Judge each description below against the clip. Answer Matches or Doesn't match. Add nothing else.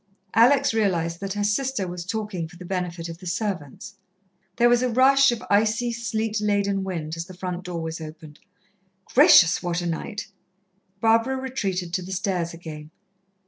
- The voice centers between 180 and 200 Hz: Matches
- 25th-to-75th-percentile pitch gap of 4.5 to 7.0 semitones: Matches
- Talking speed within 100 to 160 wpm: Doesn't match